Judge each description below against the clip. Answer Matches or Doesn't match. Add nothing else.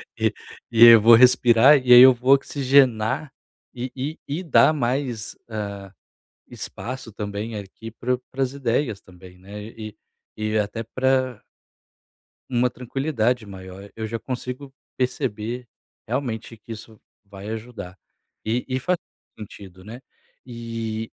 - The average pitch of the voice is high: Doesn't match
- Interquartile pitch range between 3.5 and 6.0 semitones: Doesn't match